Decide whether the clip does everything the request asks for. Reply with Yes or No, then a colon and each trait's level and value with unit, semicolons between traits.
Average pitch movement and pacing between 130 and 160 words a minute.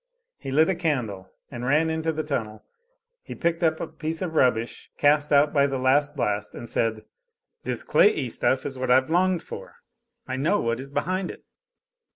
No: average, 4.0 semitones; average, 190 wpm